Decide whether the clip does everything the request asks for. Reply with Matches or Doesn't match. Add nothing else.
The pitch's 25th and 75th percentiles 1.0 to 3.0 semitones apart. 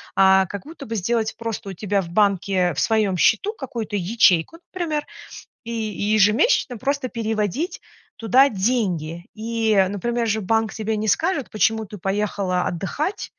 Doesn't match